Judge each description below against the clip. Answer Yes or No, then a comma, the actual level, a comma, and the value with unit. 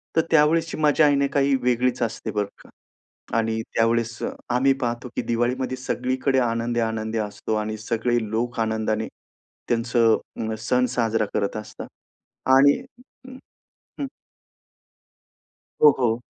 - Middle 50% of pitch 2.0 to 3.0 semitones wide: Yes, narrow, 2.6 semitones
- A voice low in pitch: Yes, low, 120 Hz